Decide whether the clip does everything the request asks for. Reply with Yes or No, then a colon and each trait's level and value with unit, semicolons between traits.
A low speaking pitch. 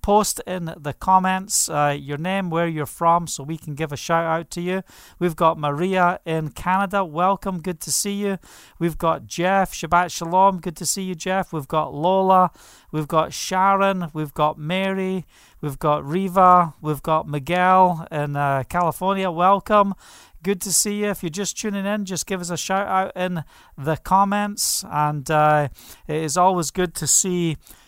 No: medium, 175 Hz